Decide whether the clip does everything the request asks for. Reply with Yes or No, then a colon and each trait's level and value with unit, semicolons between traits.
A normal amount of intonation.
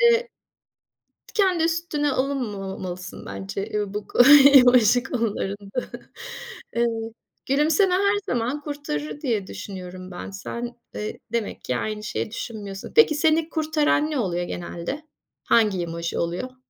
No: wide, 7.5 semitones